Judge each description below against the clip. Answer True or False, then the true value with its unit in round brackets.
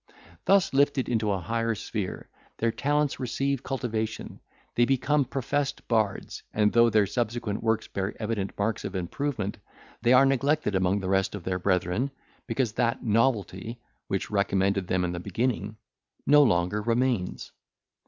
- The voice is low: True (110 Hz)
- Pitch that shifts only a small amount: False (4.5 semitones)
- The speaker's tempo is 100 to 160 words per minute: True (150 wpm)